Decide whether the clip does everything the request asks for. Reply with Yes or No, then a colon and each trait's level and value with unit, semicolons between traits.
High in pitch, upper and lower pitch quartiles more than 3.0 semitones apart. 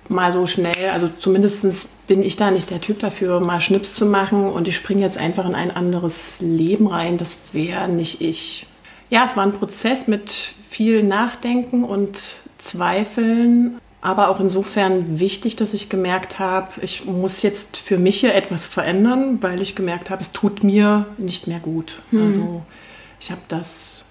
No: high, 195 Hz; average, 2.7 semitones